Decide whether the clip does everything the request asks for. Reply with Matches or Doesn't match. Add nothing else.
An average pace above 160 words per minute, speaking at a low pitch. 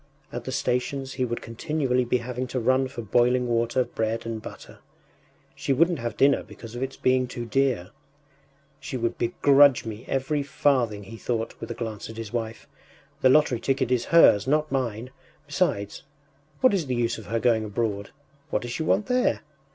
Matches